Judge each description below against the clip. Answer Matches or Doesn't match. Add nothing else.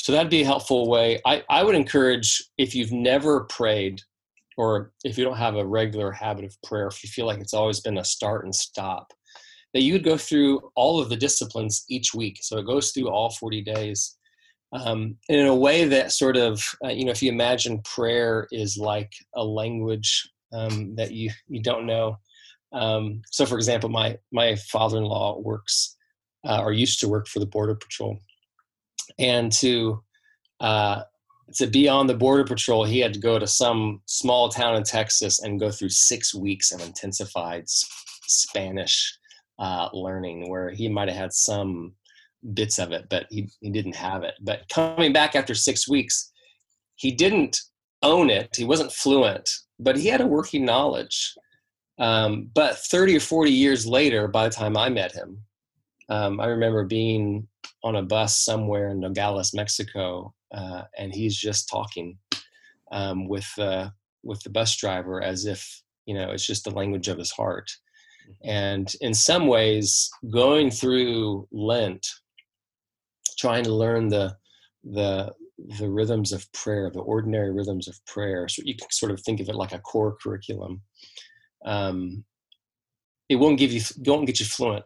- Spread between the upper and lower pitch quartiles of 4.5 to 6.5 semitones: Doesn't match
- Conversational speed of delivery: Matches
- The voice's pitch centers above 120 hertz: Doesn't match